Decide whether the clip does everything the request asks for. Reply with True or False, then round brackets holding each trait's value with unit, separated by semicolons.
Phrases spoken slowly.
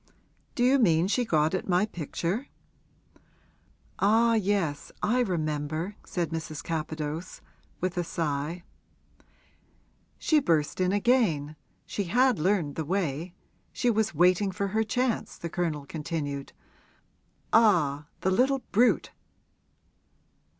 True (115 wpm)